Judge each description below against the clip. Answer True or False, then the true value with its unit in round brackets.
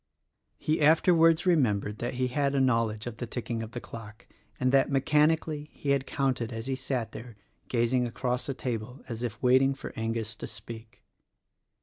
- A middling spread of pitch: True (3.3 semitones)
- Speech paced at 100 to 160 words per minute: False (180 wpm)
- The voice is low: True (125 Hz)